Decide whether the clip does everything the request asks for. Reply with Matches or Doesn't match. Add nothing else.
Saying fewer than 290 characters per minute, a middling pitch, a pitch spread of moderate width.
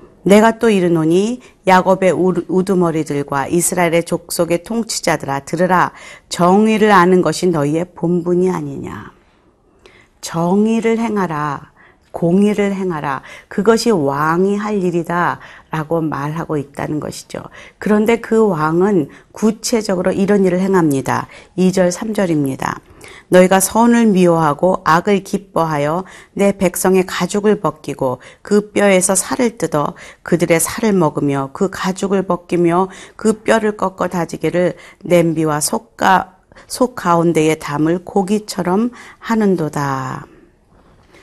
Matches